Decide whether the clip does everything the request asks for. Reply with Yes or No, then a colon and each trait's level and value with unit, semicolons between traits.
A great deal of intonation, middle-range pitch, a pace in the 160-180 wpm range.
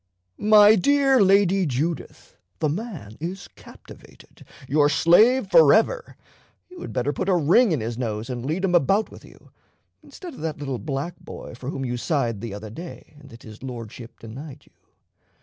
Yes: wide, 7.7 semitones; medium, 150 Hz; average, 175 wpm